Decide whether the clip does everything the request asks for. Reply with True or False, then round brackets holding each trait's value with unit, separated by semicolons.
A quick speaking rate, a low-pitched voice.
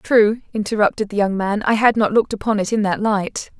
False (235 wpm; 210 Hz)